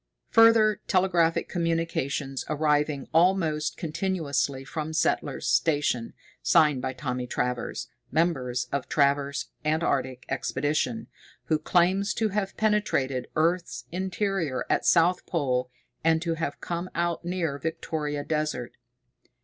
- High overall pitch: No, medium, 155 Hz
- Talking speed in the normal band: No, slow, 110 wpm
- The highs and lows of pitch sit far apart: No, average, 3.9 semitones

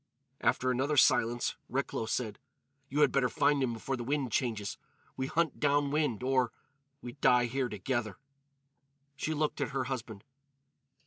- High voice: No, low, 130 Hz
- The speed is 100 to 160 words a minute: Yes, average, 145 wpm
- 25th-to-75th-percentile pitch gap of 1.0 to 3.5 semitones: Yes, average, 2.8 semitones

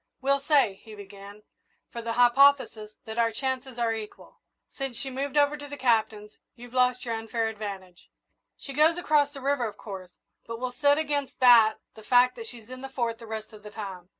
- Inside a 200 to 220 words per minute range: Yes, fast, 205 wpm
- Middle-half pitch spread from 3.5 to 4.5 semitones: Yes, average, 3.9 semitones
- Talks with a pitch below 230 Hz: No, high, 240 Hz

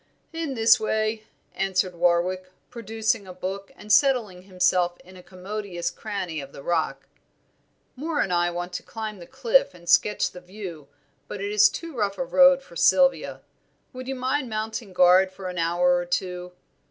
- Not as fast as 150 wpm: No, average, 175 wpm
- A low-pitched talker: No, high, 190 Hz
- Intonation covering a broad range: No, average, 3.8 semitones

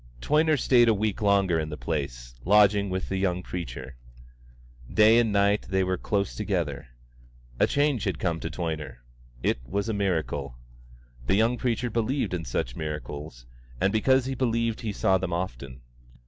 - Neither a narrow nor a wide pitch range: No, wide, 6.1 semitones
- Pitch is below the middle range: Yes, very low, 95 Hz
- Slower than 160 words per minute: No, average, 165 wpm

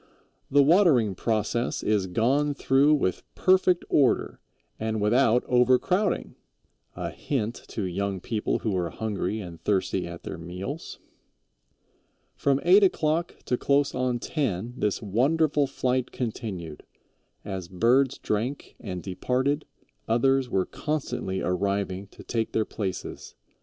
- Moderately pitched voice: No, low, 115 Hz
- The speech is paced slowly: Yes, slow, 125 wpm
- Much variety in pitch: Yes, wide, 6.1 semitones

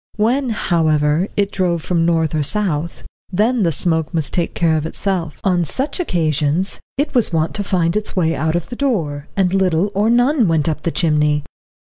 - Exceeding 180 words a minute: Yes, average, 190 wpm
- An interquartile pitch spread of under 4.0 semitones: No, average, 4.4 semitones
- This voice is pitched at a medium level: Yes, medium, 170 Hz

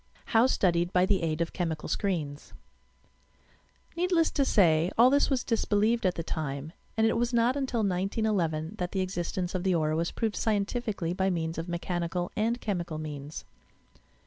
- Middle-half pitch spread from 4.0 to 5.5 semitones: Yes, average, 5.0 semitones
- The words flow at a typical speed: Yes, average, 170 wpm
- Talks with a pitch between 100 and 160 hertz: No, medium, 185 Hz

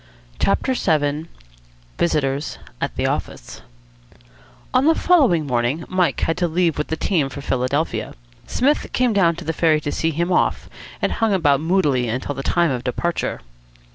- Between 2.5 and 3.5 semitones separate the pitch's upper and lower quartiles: No, average, 4.3 semitones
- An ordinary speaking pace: Yes, average, 165 wpm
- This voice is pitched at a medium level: Yes, medium, 160 Hz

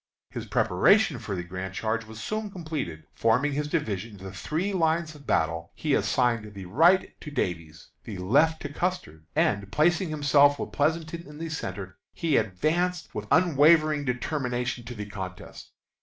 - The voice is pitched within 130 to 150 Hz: Yes, medium, 140 Hz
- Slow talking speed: No, average, 160 wpm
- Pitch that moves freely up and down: Yes, wide, 8.0 semitones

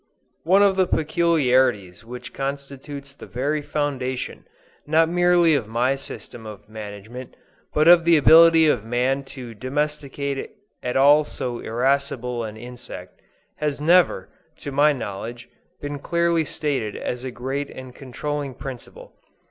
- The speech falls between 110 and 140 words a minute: Yes, slow, 135 wpm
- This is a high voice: No, low, 135 Hz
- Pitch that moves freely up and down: No, average, 3.6 semitones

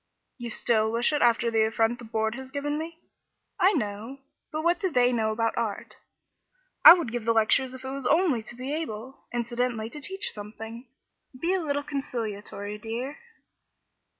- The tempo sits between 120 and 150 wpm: No, average, 180 wpm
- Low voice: No, high, 240 Hz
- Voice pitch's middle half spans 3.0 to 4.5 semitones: Yes, average, 4.2 semitones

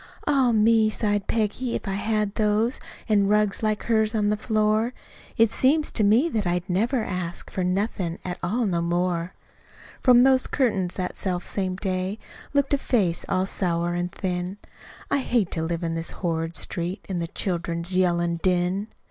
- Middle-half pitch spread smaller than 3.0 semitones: No, average, 3.7 semitones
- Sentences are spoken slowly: No, average, 175 wpm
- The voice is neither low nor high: No, high, 195 Hz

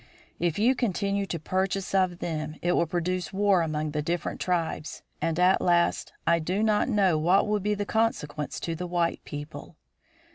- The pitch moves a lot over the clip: No, average, 3.3 semitones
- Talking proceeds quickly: No, average, 180 wpm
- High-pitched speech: No, medium, 175 Hz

